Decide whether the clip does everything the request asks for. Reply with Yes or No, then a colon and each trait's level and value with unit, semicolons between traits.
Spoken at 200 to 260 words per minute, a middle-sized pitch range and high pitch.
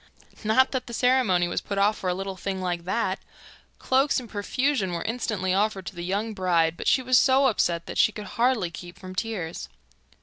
Yes: fast, 205 wpm; average, 4.7 semitones; high, 200 Hz